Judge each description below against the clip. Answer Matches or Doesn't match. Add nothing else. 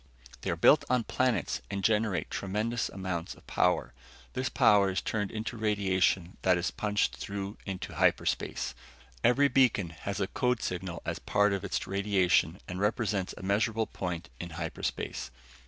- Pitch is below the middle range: Matches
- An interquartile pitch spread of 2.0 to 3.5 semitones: Matches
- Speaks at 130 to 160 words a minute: Matches